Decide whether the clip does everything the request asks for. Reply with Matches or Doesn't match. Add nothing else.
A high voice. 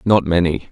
Doesn't match